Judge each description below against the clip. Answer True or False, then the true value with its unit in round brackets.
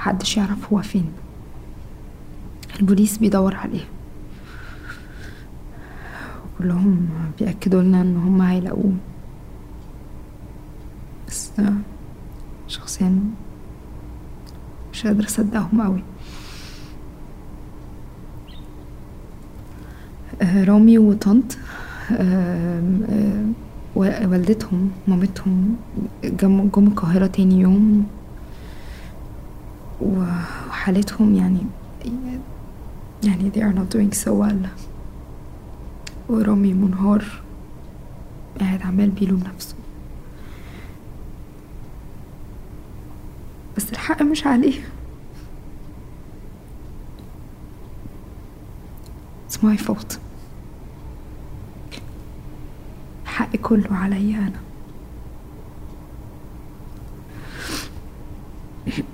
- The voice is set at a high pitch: True (195 Hz)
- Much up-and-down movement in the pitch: False (2.4 semitones)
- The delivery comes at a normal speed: False (55 wpm)